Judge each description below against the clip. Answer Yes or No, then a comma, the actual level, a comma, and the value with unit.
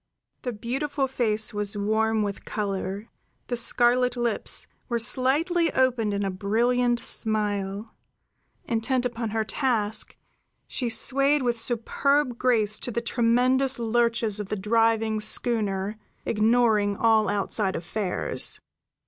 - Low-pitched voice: No, high, 225 Hz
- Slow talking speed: Yes, slow, 120 wpm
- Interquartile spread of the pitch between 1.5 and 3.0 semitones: Yes, average, 2.7 semitones